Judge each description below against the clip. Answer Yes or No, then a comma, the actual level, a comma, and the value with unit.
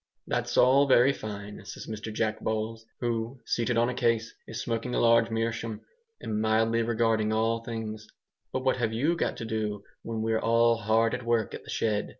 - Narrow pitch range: Yes, narrow, 1.1 semitones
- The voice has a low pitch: Yes, low, 115 Hz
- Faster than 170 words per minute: Yes, average, 190 wpm